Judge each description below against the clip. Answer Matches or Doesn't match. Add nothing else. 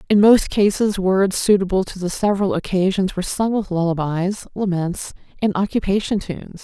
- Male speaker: Doesn't match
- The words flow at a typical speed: Matches